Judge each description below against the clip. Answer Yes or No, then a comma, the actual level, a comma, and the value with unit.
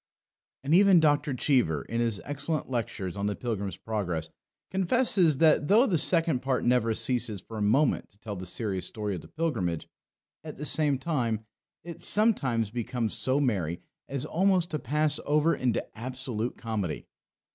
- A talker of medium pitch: No, low, 125 Hz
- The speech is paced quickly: No, average, 165 wpm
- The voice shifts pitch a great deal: Yes, wide, 6.1 semitones